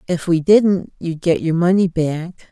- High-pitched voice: No, medium, 175 Hz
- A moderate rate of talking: Yes, average, 190 wpm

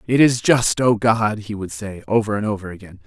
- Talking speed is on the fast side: Yes, fast, 235 wpm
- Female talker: No, male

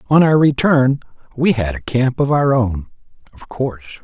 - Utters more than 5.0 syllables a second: No, 4.9 syllables/s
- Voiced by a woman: No, male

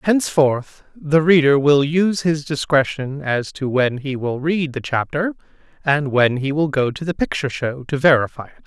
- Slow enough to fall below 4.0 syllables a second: No, 4.8 syllables/s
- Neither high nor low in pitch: Yes, medium, 145 Hz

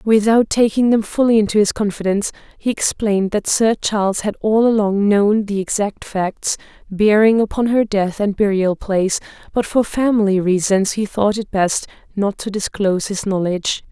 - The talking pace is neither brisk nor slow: Yes, average, 170 wpm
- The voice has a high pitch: Yes, high, 205 Hz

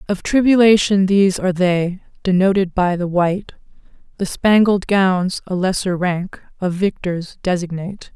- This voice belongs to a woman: Yes, female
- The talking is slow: Yes, slow, 130 wpm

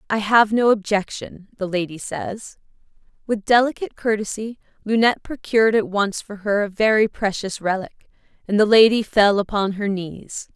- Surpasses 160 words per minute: No, average, 155 wpm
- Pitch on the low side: No, high, 210 Hz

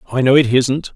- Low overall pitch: Yes, low, 130 Hz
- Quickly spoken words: Yes, fast, 250 wpm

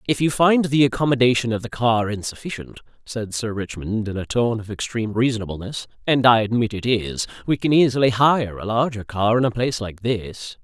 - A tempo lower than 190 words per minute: No, average, 195 wpm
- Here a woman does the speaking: No, male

